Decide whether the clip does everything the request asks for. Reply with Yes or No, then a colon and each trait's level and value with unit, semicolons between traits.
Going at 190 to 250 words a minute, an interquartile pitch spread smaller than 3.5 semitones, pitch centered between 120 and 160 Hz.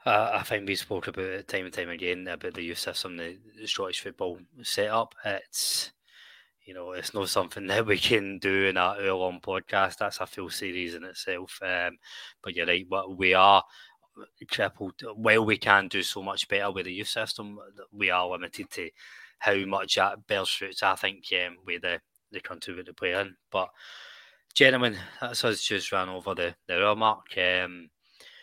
No: average, 195 wpm; narrow, 2.5 semitones; very low, 95 Hz